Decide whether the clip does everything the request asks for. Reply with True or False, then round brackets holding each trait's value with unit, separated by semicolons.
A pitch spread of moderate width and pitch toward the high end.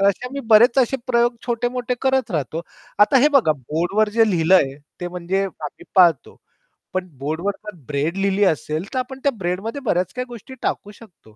False (6.0 semitones; 200 Hz)